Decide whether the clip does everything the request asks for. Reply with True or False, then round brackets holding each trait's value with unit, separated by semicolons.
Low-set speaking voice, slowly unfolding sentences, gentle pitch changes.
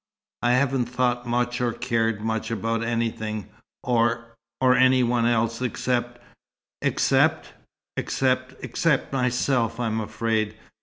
True (120 Hz; 120 wpm; 1.7 semitones)